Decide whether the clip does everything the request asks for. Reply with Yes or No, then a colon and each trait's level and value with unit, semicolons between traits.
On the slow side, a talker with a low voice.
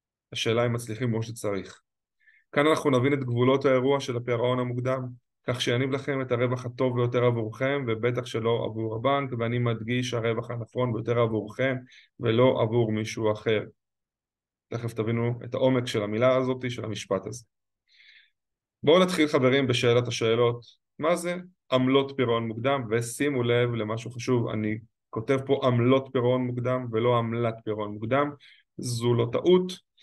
No: average, 145 wpm; low, 120 Hz